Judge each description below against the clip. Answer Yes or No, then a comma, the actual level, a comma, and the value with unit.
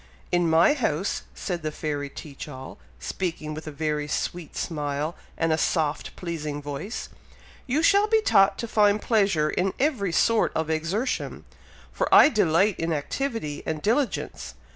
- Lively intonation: Yes, wide, 5.8 semitones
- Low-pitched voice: No, medium, 165 Hz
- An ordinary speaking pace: Yes, average, 155 wpm